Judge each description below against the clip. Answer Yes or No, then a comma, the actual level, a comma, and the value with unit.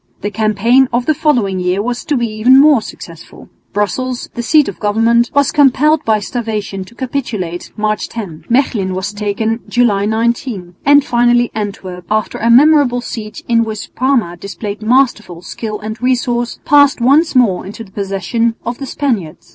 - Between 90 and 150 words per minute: No, average, 165 wpm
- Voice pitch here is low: No, high, 230 Hz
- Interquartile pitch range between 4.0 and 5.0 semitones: No, average, 3.6 semitones